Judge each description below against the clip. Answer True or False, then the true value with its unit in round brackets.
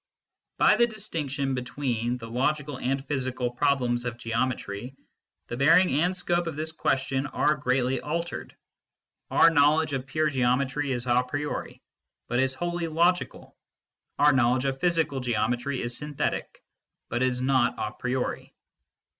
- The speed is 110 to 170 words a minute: True (145 wpm)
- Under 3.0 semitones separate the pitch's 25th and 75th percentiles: False (3.4 semitones)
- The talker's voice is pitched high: False (135 Hz)